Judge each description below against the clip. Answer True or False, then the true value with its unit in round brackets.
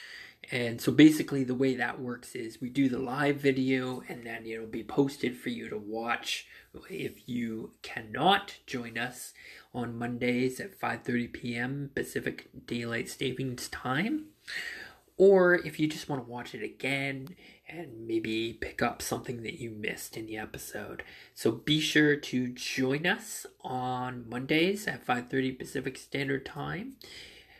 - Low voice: True (130 Hz)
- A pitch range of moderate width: True (3.8 semitones)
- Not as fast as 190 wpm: True (150 wpm)